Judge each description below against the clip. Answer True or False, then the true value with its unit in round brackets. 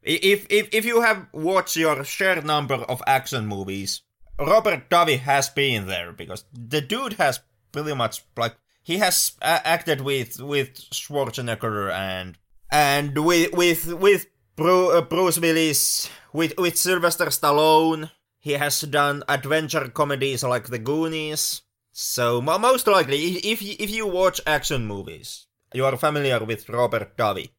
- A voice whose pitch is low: False (145 Hz)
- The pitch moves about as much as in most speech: False (5.9 semitones)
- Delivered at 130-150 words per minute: True (140 wpm)